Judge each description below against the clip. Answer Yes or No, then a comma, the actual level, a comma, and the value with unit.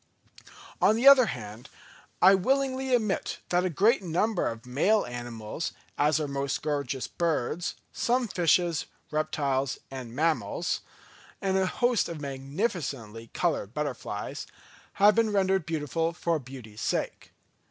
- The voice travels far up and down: Yes, wide, 6.6 semitones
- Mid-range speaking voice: Yes, medium, 160 Hz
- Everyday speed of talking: No, slow, 130 wpm